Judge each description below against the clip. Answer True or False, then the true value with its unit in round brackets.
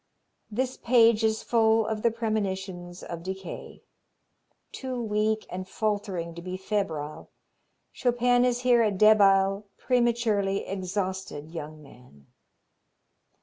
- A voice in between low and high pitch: False (205 Hz)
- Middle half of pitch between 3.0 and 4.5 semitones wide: True (3.6 semitones)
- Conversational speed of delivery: False (110 wpm)